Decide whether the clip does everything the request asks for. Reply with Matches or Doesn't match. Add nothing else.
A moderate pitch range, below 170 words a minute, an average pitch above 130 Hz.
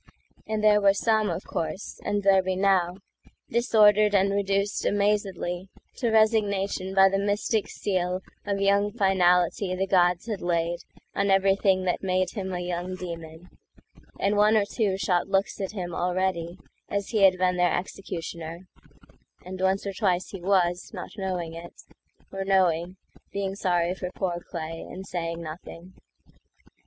Doesn't match